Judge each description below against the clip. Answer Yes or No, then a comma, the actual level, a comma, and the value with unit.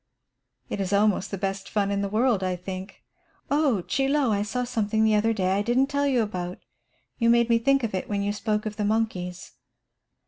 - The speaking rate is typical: No, fast, 215 wpm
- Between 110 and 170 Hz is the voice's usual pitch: No, high, 210 Hz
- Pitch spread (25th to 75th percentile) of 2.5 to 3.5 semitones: Yes, average, 3.1 semitones